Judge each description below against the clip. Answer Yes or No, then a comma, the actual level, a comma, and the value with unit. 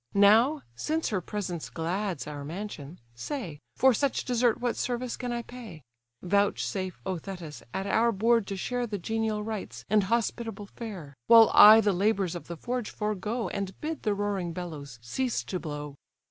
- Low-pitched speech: No, high, 205 Hz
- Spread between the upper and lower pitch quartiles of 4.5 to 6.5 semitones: Yes, average, 4.8 semitones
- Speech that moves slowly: No, average, 170 wpm